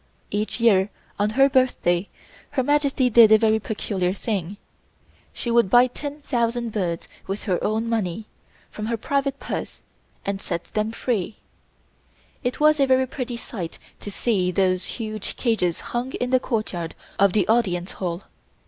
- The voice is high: Yes, high, 220 Hz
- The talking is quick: No, average, 155 wpm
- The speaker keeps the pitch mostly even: No, average, 4.3 semitones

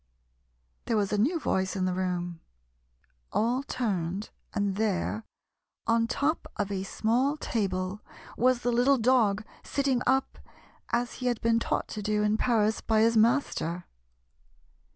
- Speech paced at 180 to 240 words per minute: No, average, 145 wpm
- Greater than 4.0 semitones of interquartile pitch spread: No, average, 3.6 semitones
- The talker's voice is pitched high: Yes, high, 220 Hz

